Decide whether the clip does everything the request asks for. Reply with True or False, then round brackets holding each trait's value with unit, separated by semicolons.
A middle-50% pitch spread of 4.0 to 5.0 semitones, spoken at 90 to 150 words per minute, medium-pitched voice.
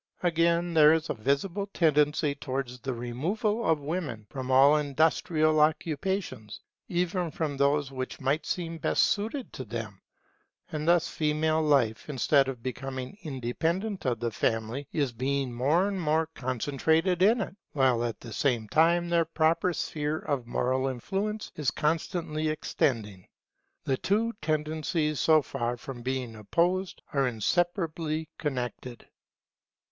True (4.4 semitones; 140 wpm; 150 Hz)